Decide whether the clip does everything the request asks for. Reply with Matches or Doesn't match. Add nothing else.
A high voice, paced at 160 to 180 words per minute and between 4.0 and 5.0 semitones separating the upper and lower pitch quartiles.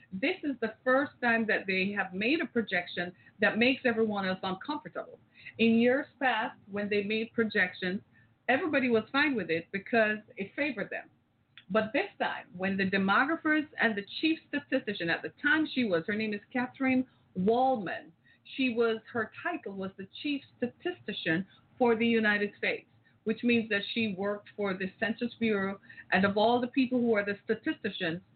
Matches